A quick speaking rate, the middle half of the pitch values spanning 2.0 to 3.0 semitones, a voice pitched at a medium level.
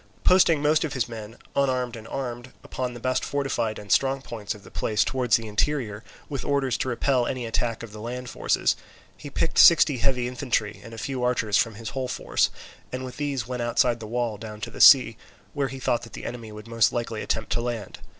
No: fast, 220 wpm; average, 2.7 semitones; low, 120 Hz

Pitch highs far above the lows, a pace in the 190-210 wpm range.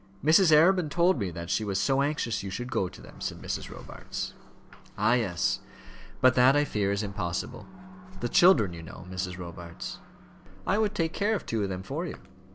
Yes: wide, 8.8 semitones; average, 195 wpm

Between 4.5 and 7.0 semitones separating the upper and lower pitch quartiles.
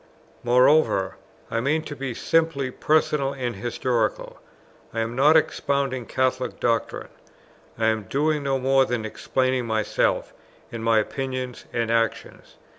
No: average, 3.2 semitones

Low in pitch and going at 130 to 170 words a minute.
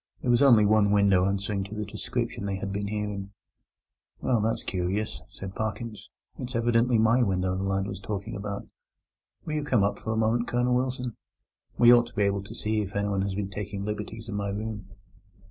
No: low, 105 Hz; average, 200 wpm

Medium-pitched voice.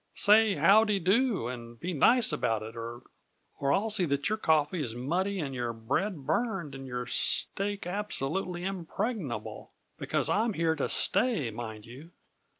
Yes: medium, 160 Hz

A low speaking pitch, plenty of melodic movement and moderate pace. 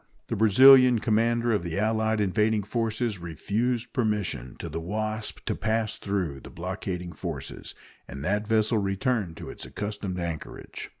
No: low, 105 Hz; average, 3.6 semitones; average, 145 wpm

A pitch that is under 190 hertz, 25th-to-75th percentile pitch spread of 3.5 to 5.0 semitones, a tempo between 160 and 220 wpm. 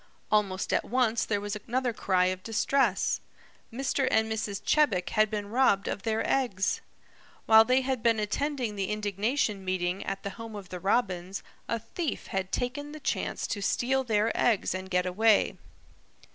No: high, 215 Hz; average, 4.0 semitones; average, 170 wpm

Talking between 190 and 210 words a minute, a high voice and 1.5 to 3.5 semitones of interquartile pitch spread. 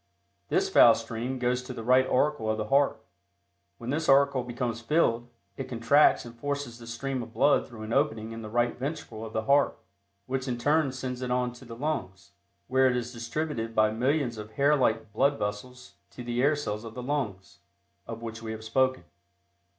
No: average, 200 wpm; low, 125 Hz; average, 3.2 semitones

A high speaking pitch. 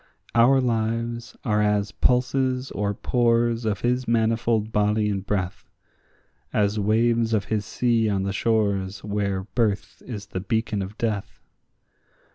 No: low, 110 Hz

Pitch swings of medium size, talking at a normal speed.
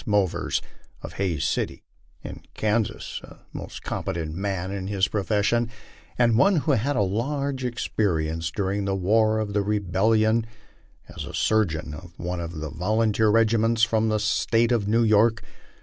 Yes: average, 3.2 semitones; average, 150 wpm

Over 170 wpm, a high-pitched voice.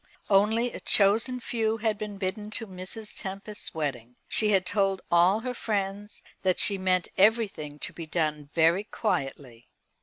No: average, 155 wpm; high, 195 Hz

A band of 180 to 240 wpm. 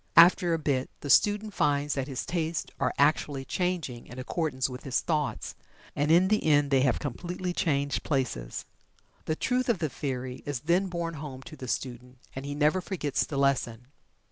Yes: average, 185 wpm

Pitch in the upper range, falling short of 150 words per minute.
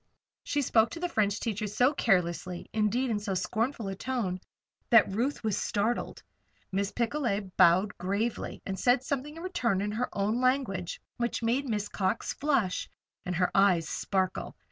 No: high, 215 Hz; average, 165 wpm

